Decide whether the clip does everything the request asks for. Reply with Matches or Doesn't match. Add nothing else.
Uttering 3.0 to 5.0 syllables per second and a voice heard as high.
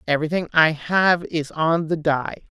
Doesn't match